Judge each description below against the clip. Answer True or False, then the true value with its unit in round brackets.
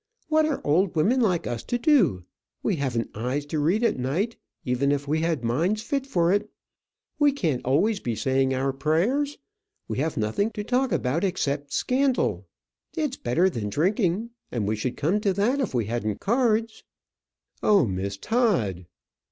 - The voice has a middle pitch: True (165 Hz)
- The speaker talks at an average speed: True (170 wpm)